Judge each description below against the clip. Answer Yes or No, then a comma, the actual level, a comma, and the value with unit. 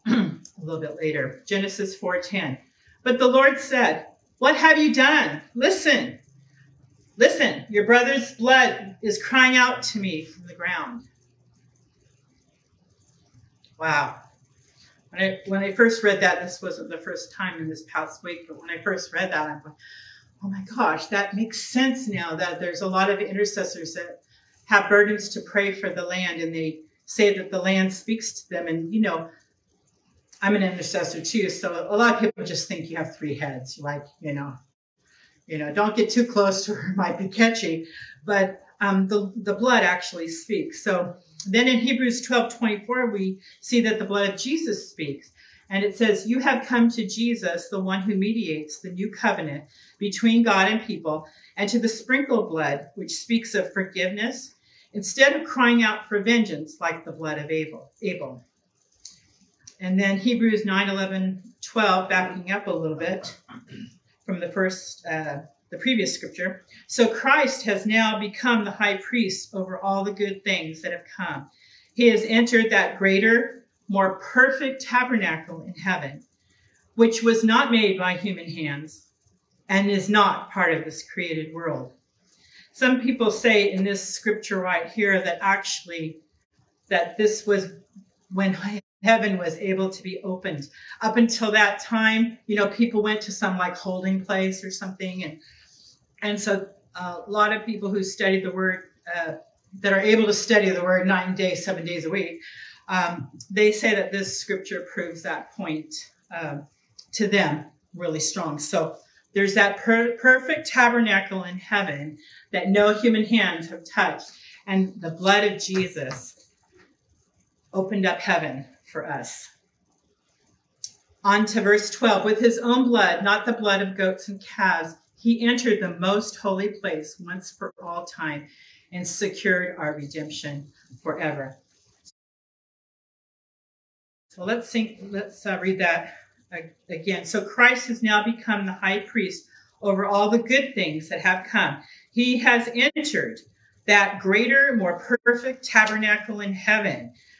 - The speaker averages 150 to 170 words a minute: Yes, average, 160 wpm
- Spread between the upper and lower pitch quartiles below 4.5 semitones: Yes, average, 4.1 semitones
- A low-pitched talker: No, high, 195 Hz